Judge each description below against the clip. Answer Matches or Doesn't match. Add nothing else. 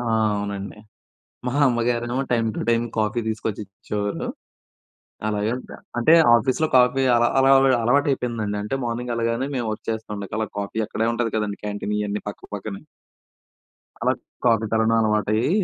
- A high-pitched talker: Doesn't match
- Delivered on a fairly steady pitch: Matches